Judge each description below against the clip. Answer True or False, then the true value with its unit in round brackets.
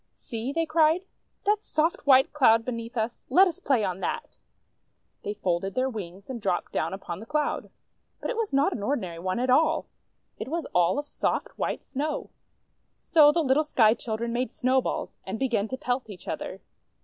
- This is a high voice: True (255 Hz)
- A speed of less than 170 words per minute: False (190 wpm)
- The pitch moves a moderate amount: False (5.8 semitones)